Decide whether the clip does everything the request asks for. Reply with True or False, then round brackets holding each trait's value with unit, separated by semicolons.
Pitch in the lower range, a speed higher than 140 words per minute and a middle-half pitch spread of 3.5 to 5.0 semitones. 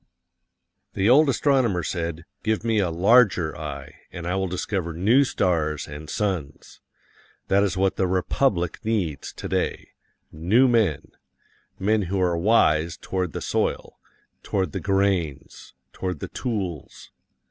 False (95 Hz; 135 wpm; 4.2 semitones)